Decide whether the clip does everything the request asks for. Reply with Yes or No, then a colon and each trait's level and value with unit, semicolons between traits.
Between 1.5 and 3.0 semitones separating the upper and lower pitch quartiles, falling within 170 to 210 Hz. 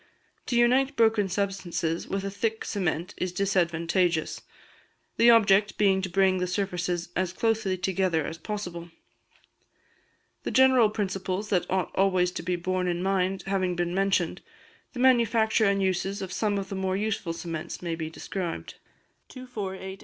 Yes: narrow, 2.5 semitones; high, 190 Hz